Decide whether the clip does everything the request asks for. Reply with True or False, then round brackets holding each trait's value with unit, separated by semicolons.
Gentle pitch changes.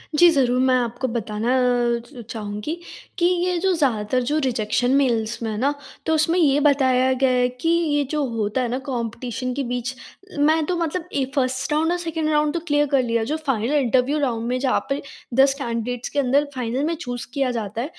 False (3.9 semitones)